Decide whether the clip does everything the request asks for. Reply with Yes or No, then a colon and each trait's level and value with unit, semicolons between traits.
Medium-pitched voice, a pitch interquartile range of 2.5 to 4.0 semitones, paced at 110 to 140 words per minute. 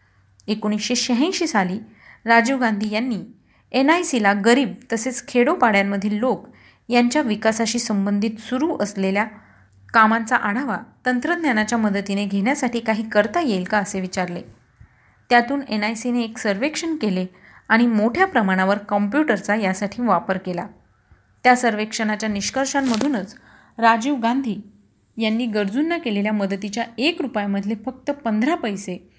No: high, 220 Hz; average, 3.4 semitones; average, 115 wpm